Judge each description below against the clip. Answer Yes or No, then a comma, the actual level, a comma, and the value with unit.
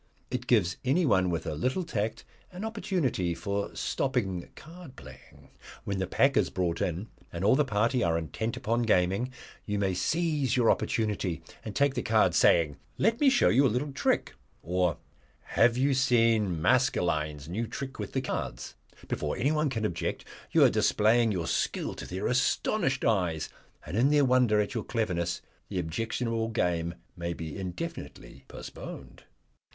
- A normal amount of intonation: No, wide, 6.6 semitones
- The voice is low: Yes, low, 110 Hz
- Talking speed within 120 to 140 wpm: No, average, 165 wpm